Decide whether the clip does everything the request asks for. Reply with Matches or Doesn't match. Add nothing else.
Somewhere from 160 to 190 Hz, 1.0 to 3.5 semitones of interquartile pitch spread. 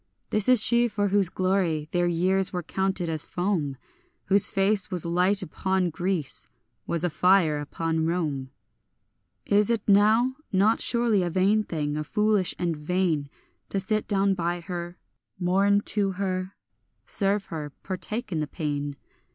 Matches